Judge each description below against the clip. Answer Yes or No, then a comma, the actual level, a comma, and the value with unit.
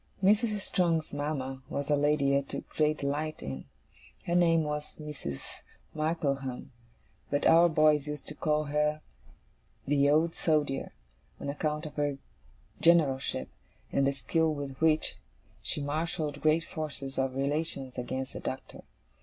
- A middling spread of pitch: No, narrow, 2.1 semitones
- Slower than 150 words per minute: Yes, average, 140 wpm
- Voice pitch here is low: No, medium, 150 Hz